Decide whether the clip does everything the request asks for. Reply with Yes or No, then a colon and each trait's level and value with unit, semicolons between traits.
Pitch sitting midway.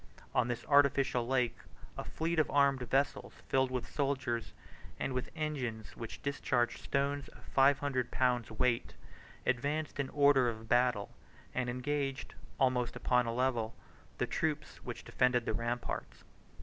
No: low, 130 Hz